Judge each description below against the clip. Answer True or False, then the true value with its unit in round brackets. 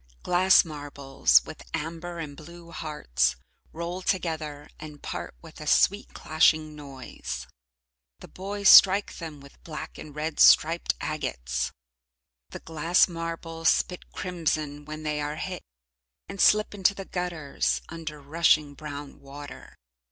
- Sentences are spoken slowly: True (130 wpm)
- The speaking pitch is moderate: True (155 Hz)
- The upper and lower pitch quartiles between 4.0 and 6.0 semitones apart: False (2.7 semitones)